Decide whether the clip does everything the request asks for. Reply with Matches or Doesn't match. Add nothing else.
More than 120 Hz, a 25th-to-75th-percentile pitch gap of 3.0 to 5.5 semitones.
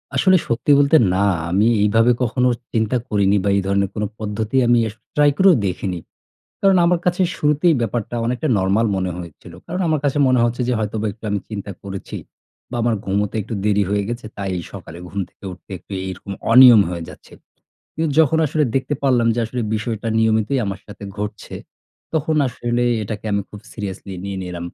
Doesn't match